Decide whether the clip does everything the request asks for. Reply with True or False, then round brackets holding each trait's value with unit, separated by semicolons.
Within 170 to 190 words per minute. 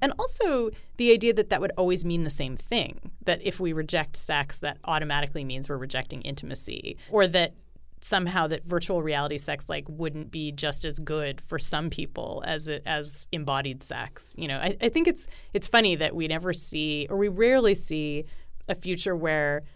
True (180 wpm)